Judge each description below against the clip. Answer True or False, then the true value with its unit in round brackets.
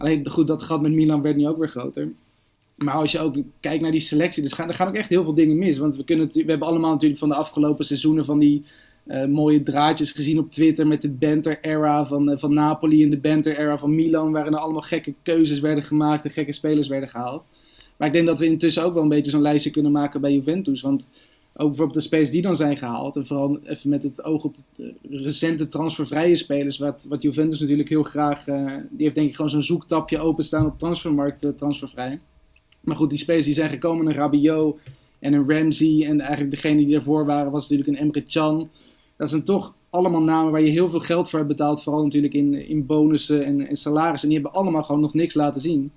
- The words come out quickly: True (235 wpm)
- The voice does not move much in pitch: True (1.3 semitones)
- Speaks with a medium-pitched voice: True (150 Hz)